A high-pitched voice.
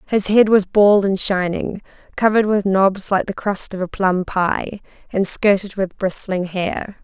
Yes: high, 195 Hz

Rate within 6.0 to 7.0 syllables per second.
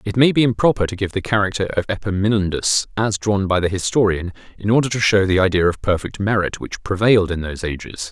Yes: 6.1 syllables/s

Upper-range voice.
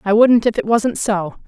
Yes: high, 215 Hz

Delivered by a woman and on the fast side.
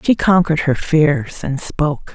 No: female; average, 170 wpm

